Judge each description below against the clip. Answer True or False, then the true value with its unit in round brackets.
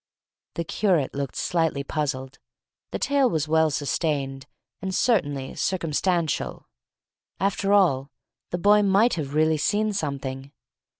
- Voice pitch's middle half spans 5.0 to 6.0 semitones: True (5.6 semitones)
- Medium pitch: True (160 Hz)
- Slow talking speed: True (120 wpm)